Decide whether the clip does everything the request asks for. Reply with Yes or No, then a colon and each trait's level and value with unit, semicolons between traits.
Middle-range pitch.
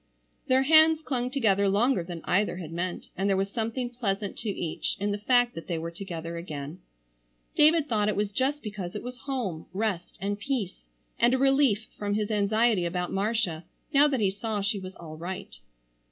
No: high, 205 Hz